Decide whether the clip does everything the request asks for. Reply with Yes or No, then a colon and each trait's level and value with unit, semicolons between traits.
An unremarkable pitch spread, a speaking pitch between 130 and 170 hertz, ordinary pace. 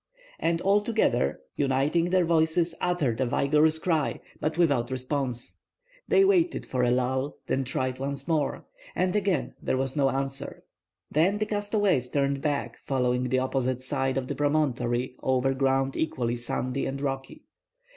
Yes: average, 3.8 semitones; low, 135 Hz; average, 155 wpm